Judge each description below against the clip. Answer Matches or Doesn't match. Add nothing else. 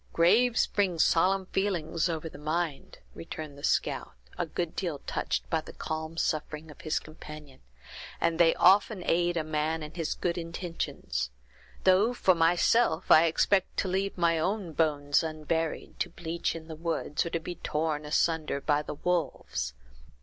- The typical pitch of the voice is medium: Matches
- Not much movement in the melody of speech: Matches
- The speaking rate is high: Doesn't match